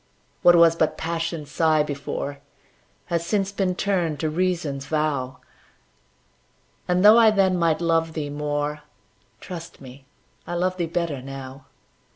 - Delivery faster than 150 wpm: No, average, 140 wpm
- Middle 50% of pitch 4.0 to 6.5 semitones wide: No, average, 3.3 semitones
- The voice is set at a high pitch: No, medium, 165 Hz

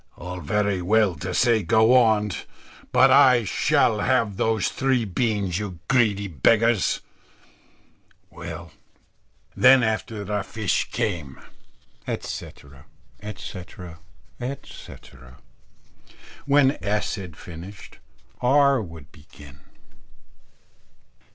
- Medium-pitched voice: No, low, 105 Hz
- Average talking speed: No, slow, 100 wpm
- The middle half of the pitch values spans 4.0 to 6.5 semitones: Yes, average, 4.6 semitones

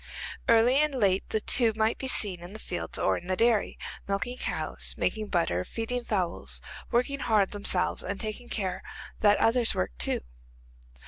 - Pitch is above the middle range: Yes, high, 215 Hz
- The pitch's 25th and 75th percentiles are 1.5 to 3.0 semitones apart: No, average, 3.9 semitones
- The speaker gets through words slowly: No, average, 170 wpm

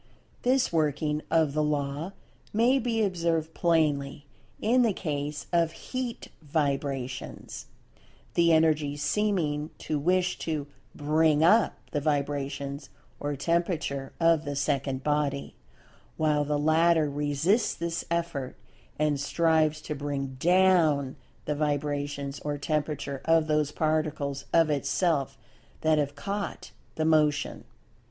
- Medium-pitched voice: Yes, medium, 150 Hz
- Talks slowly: Yes, slow, 115 wpm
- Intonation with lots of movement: No, narrow, 2.5 semitones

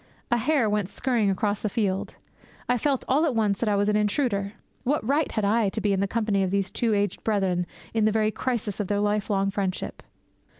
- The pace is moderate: No, fast, 220 wpm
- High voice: Yes, high, 210 Hz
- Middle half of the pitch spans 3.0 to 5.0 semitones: No, narrow, 2.5 semitones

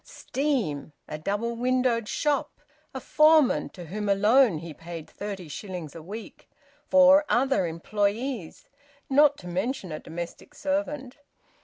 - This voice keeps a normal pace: No, slow, 130 wpm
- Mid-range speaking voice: No, high, 215 Hz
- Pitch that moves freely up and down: Yes, wide, 7.7 semitones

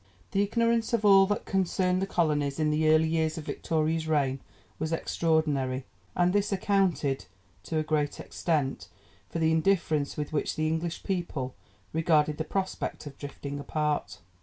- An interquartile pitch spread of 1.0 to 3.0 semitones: No, average, 3.5 semitones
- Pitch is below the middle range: No, medium, 160 Hz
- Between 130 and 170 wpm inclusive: Yes, average, 160 wpm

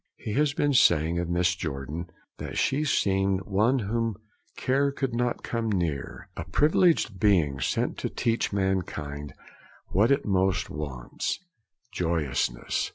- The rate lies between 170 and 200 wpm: No, slow, 135 wpm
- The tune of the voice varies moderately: No, wide, 6.4 semitones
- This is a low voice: Yes, very low, 95 Hz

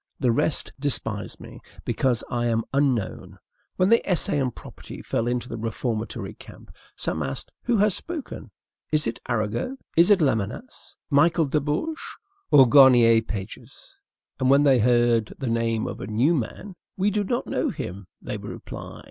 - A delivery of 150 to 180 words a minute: Yes, average, 165 wpm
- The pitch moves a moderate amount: No, wide, 5.7 semitones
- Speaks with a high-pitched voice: No, low, 125 Hz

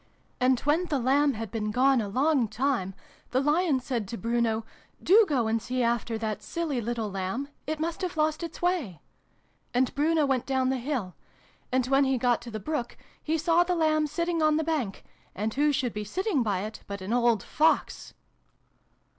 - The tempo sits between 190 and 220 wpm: Yes, average, 195 wpm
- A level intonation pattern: No, average, 5.3 semitones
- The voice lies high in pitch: Yes, very high, 260 Hz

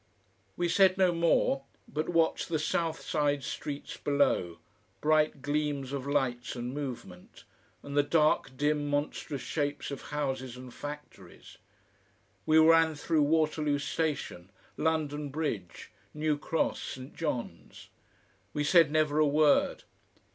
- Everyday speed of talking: No, slow, 125 wpm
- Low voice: No, medium, 145 Hz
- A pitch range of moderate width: No, narrow, 2.2 semitones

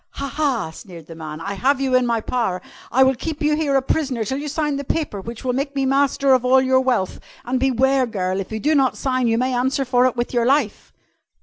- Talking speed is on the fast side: Yes, fast, 250 wpm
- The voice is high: Yes, very high, 255 Hz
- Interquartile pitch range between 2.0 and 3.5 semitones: Yes, average, 3.0 semitones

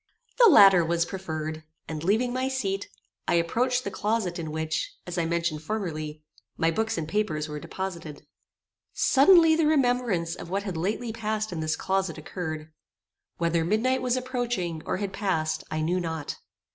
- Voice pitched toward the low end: No, medium, 185 Hz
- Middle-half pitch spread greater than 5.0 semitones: Yes, wide, 5.6 semitones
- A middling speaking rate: Yes, average, 165 wpm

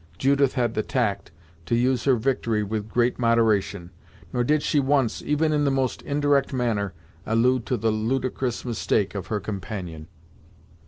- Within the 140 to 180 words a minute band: Yes, average, 160 wpm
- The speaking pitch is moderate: No, low, 120 Hz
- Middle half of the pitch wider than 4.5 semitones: No, average, 3.8 semitones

